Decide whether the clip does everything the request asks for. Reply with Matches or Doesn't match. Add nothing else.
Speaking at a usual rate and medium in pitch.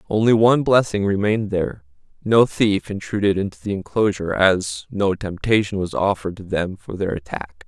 Doesn't match